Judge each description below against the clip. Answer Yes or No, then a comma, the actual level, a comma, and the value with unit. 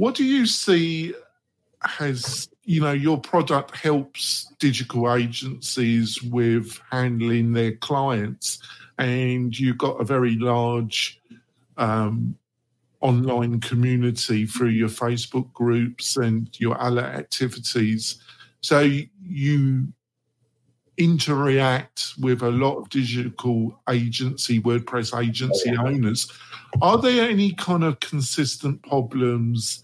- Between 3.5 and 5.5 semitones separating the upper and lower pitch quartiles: No, average, 2.9 semitones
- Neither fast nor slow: No, slow, 105 wpm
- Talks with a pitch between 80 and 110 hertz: No, low, 125 Hz